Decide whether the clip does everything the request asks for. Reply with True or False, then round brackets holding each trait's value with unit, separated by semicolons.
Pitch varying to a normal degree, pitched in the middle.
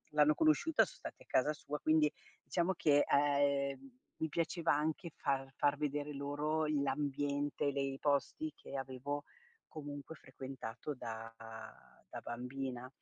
False (2.0 semitones; 145 Hz)